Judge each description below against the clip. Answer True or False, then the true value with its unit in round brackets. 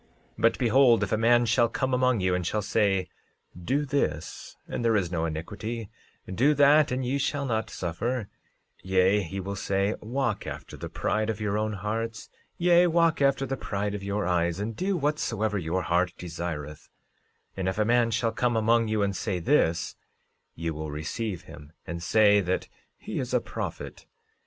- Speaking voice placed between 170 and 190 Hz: False (105 Hz)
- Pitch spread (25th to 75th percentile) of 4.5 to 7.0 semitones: True (4.8 semitones)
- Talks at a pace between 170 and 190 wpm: True (180 wpm)